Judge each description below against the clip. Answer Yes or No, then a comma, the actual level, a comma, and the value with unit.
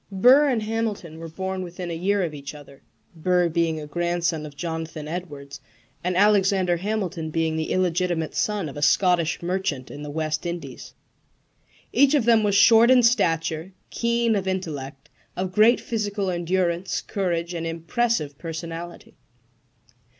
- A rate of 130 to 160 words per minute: Yes, average, 150 wpm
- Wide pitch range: No, average, 3.7 semitones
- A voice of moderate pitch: Yes, medium, 175 Hz